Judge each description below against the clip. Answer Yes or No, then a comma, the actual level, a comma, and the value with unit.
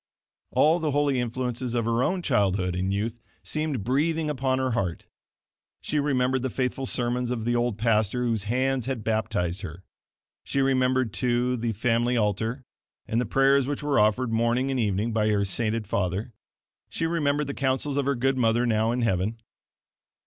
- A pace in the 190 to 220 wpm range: No, average, 175 wpm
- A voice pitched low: Yes, low, 120 Hz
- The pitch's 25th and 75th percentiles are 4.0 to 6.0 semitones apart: No, average, 3.4 semitones